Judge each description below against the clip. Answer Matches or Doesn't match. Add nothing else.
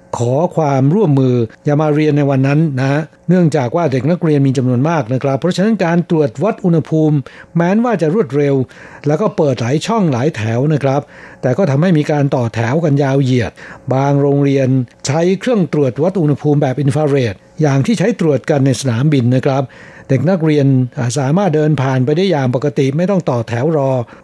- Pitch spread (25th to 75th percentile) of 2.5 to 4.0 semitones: Matches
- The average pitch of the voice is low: Doesn't match